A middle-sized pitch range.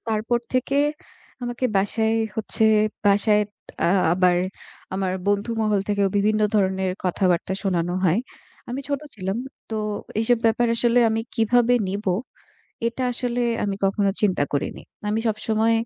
Yes: average, 3.0 semitones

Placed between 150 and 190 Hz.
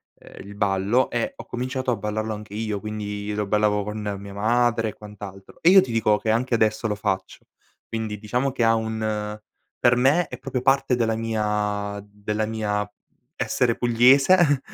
No: low, 110 Hz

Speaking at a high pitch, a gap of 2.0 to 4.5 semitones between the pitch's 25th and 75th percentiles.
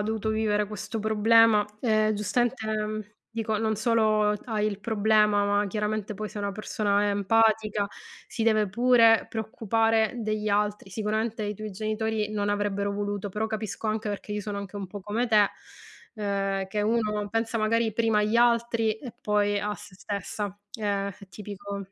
No: high, 210 Hz; narrow, 1.3 semitones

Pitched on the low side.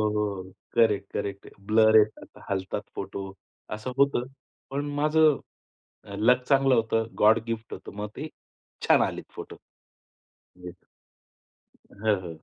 Yes: low, 110 Hz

